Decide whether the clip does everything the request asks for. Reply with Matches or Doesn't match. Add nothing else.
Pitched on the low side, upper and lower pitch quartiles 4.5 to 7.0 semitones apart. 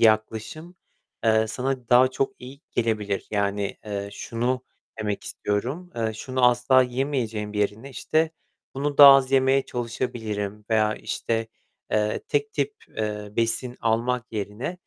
Doesn't match